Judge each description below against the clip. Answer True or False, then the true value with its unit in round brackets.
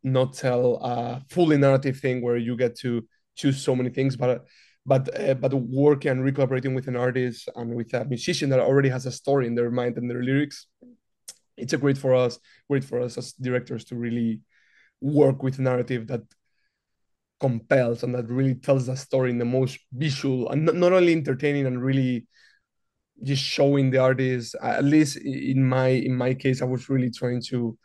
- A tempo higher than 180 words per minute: True (190 wpm)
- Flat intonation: True (1.7 semitones)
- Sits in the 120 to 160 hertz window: True (130 Hz)